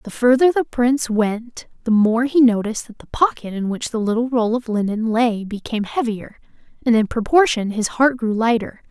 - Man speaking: No, female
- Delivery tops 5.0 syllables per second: Yes, 5.2 syllables/s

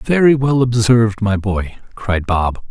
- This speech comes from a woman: No, male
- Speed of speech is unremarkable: Yes, average, 155 wpm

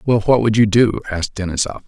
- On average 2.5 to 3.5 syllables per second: No, 6.5 syllables/s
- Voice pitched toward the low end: Yes, low, 105 Hz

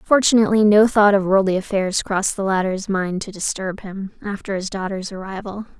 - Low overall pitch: No, high, 195 Hz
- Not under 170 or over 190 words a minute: Yes, average, 175 wpm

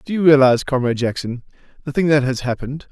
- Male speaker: Yes, male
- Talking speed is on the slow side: No, fast, 205 wpm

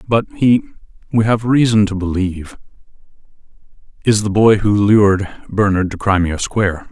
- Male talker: Yes, male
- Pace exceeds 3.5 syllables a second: Yes, 5.0 syllables/s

